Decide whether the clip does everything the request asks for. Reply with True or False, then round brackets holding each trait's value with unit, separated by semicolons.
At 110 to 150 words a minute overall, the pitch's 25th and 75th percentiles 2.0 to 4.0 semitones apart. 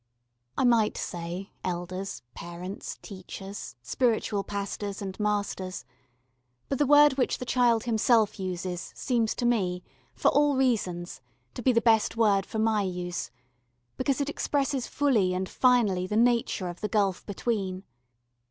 False (145 wpm; 4.6 semitones)